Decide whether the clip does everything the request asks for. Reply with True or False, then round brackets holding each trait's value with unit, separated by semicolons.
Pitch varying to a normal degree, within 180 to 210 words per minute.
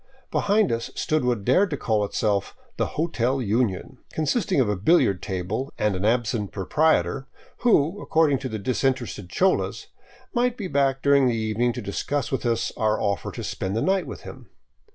False (6.3 semitones; 185 wpm)